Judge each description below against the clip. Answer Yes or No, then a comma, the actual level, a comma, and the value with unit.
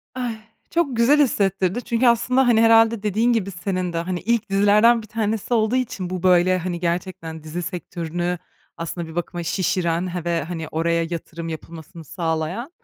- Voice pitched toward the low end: No, medium, 185 Hz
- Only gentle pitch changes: No, average, 5.0 semitones